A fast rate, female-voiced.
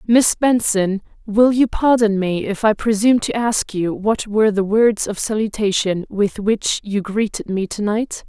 No: average, 180 wpm; female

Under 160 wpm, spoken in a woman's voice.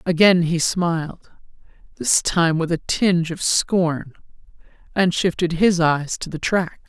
Yes: average, 150 wpm; female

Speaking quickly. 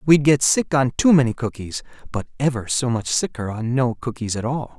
Yes: fast, 215 wpm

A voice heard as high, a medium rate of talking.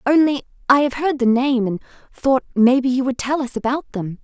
No: very high, 260 Hz; fast, 210 wpm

